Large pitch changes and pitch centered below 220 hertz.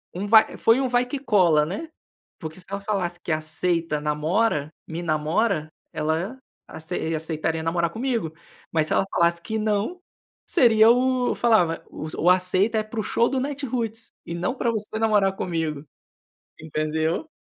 Yes: wide, 5.9 semitones; medium, 185 Hz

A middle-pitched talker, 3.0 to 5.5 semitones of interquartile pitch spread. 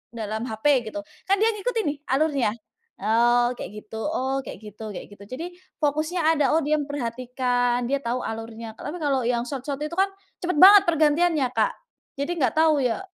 No: very high, 275 Hz; average, 4.5 semitones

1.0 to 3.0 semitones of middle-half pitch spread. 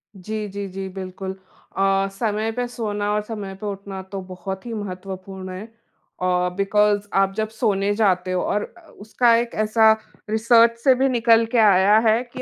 Yes: narrow, 2.5 semitones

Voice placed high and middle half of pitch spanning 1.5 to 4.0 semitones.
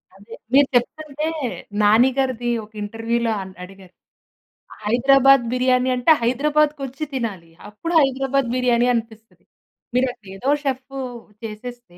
Yes: high, 245 Hz; average, 3.3 semitones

